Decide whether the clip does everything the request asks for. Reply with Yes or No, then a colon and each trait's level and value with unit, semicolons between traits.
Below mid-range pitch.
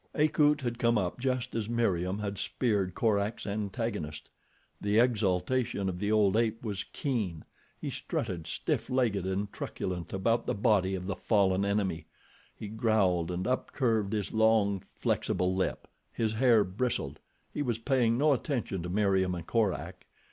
Yes: low, 105 Hz